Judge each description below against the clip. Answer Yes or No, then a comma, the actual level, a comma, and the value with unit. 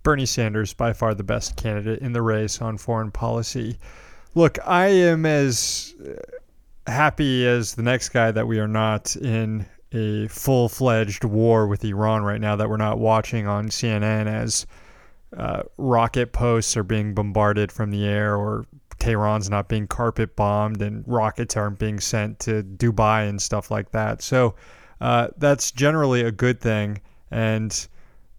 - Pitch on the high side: No, low, 110 Hz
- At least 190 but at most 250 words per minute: No, average, 160 wpm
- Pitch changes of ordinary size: No, narrow, 2.3 semitones